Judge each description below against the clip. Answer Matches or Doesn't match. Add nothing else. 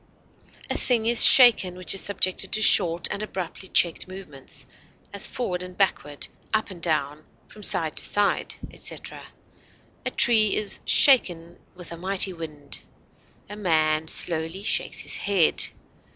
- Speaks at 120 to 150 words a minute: Matches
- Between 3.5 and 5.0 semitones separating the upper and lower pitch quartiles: Matches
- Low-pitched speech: Doesn't match